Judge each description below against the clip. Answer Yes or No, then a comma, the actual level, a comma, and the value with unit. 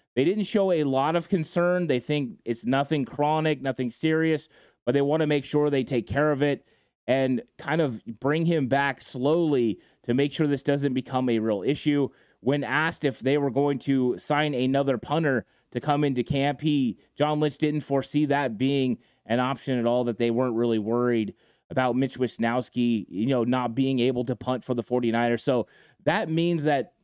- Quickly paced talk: No, average, 195 wpm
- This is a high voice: No, low, 135 Hz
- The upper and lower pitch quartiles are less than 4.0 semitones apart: Yes, average, 3.3 semitones